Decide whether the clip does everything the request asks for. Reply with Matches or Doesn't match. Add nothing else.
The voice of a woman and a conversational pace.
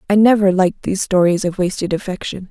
Matches